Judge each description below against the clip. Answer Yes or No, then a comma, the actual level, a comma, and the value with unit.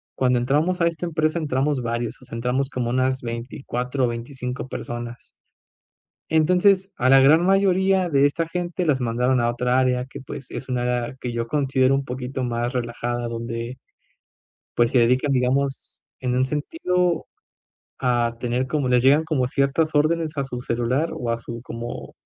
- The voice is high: No, low, 130 Hz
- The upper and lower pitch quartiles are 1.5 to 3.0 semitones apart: No, average, 3.7 semitones